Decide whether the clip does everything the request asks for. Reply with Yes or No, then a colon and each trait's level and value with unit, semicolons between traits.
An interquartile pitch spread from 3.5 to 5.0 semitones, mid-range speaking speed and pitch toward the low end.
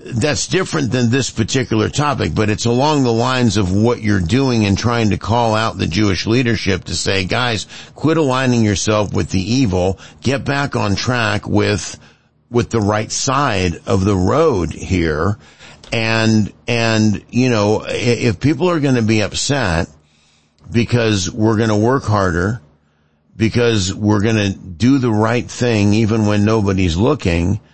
Yes: average, 3.8 semitones; average, 160 wpm; low, 110 Hz